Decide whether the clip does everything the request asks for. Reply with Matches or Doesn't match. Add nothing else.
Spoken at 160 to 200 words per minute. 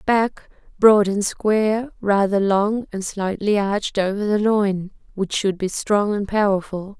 Doesn't match